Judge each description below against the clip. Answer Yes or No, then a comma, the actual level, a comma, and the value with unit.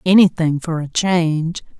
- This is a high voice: No, medium, 165 Hz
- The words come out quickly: No, slow, 135 wpm